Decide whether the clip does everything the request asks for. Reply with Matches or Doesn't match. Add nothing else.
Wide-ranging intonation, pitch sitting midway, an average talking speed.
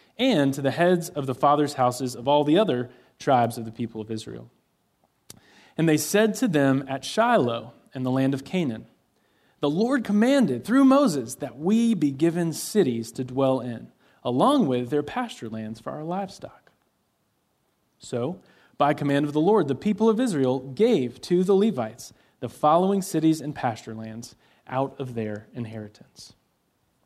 Matches